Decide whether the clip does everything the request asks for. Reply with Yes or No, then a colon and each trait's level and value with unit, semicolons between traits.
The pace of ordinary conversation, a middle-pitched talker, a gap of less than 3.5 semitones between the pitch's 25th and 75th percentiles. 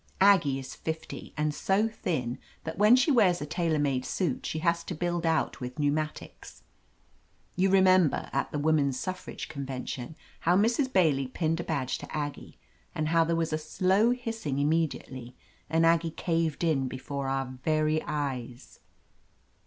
No: average, 160 wpm; medium, 160 Hz; average, 4.1 semitones